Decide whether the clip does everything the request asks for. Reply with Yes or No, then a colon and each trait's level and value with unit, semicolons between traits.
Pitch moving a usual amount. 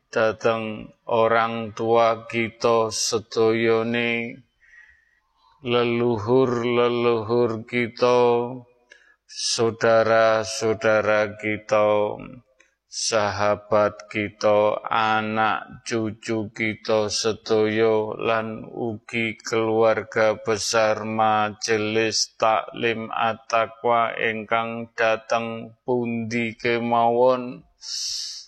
No: narrow, 1.4 semitones